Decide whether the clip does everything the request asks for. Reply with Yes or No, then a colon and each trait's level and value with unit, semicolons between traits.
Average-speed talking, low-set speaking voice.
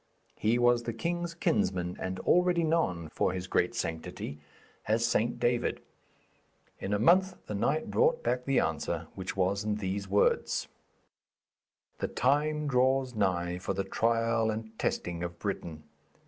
Yes: average, 145 wpm; low, 110 Hz